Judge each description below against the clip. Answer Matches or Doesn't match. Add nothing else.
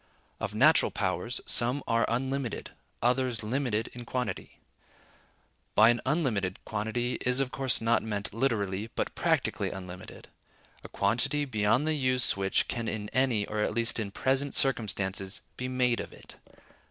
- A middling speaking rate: Matches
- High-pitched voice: Doesn't match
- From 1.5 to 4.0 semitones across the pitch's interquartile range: Matches